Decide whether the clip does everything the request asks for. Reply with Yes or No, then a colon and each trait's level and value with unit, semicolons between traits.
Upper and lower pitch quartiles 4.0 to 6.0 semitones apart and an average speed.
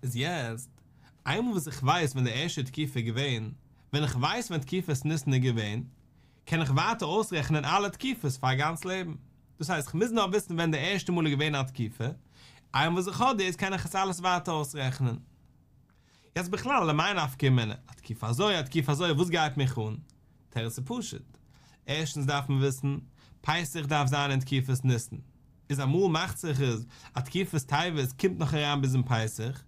Yes: average, 4.3 semitones; average, 195 wpm